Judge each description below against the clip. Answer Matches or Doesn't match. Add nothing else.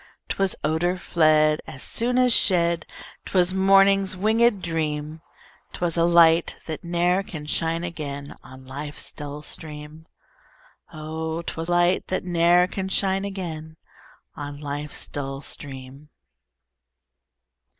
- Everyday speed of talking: Doesn't match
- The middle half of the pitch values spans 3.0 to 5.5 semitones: Matches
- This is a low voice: Doesn't match